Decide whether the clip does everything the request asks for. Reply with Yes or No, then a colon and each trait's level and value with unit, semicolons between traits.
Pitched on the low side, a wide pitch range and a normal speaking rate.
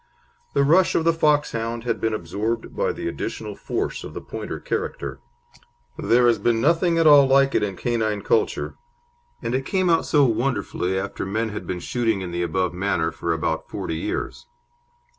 Yes: low, 115 Hz; wide, 6.5 semitones; average, 180 wpm